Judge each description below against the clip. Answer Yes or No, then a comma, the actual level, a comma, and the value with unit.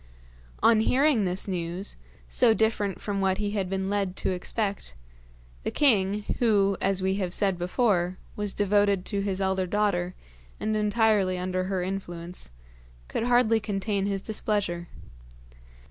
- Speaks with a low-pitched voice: No, high, 195 Hz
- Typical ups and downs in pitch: No, narrow, 2.2 semitones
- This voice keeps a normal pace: Yes, average, 145 wpm